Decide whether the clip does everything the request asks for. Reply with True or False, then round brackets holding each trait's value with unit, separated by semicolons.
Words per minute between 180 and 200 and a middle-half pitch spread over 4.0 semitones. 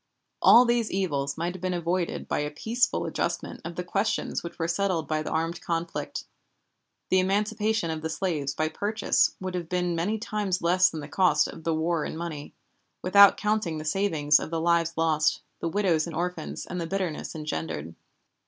False (190 wpm; 3.3 semitones)